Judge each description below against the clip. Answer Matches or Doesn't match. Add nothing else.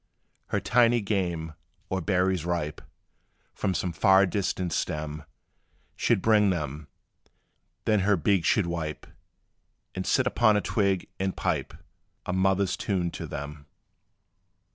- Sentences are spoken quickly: Doesn't match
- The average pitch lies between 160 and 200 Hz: Doesn't match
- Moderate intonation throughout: Matches